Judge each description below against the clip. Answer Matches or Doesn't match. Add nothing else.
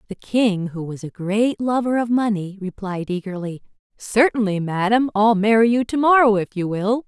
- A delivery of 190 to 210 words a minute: Doesn't match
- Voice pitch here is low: Doesn't match